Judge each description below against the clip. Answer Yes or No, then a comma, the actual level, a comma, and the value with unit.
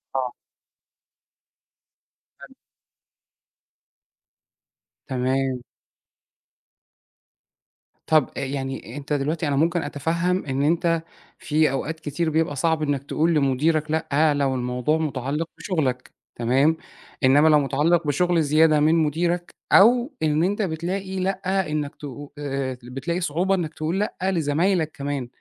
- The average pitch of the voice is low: No, medium, 155 Hz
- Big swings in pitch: No, average, 3.4 semitones